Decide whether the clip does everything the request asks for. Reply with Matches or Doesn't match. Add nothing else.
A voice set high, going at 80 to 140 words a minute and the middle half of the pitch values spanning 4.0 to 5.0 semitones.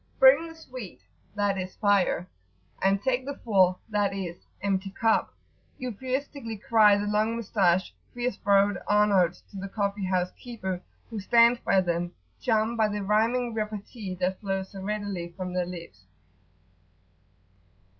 Doesn't match